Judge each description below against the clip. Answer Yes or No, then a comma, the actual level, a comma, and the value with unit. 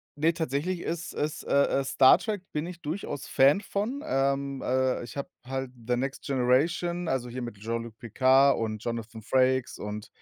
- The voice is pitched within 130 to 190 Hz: Yes, low, 135 Hz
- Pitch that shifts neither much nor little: Yes, average, 4.6 semitones